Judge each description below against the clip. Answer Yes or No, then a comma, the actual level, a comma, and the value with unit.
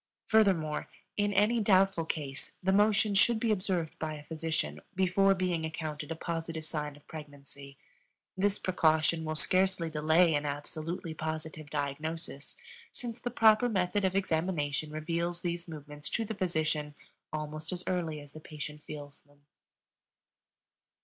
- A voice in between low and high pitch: Yes, medium, 160 Hz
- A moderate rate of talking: Yes, average, 145 wpm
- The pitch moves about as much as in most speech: Yes, average, 3.8 semitones